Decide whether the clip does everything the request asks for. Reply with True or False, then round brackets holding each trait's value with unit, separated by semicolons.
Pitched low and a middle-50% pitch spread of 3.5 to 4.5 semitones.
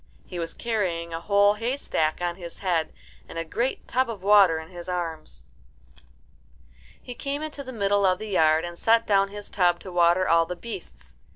False (185 Hz; 3.9 semitones)